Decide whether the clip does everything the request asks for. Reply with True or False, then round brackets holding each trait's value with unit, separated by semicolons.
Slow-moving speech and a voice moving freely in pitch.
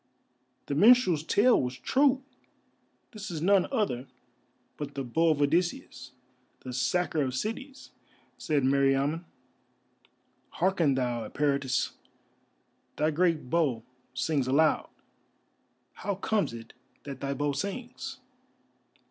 True (110 wpm; 6.0 semitones)